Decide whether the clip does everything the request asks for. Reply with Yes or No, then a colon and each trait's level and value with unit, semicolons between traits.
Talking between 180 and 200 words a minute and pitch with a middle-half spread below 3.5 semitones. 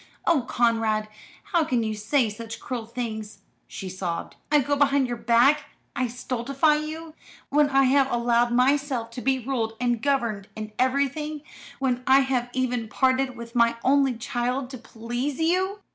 No: average, 160 wpm; average, 3.1 semitones